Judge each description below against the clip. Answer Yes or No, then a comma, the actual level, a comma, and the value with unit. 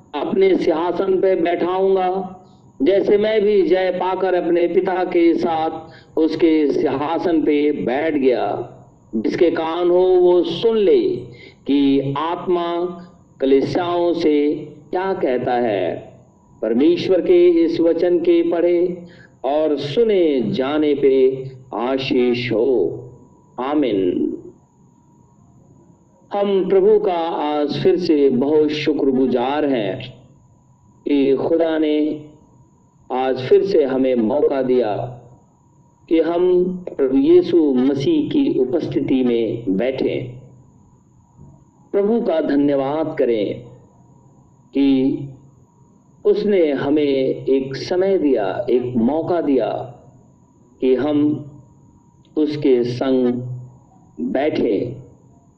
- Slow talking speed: Yes, slow, 95 wpm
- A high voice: No, medium, 160 Hz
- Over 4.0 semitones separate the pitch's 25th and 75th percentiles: Yes, average, 5.2 semitones